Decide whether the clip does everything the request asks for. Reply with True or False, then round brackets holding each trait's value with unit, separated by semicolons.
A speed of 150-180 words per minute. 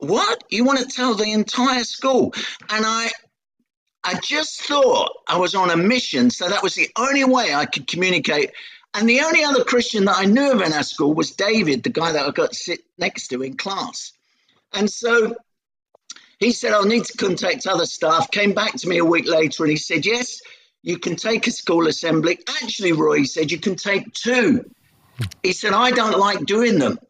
False (205 wpm)